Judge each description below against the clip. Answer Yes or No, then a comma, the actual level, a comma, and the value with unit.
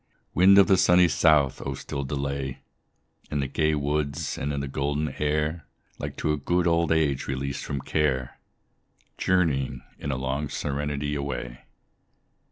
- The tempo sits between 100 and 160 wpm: Yes, average, 150 wpm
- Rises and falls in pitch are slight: Yes, narrow, 2.1 semitones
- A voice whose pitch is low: Yes, very low, 70 Hz